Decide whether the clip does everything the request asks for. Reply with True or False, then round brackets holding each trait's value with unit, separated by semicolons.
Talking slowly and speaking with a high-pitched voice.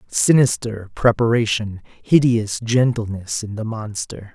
False (95 wpm; 110 Hz)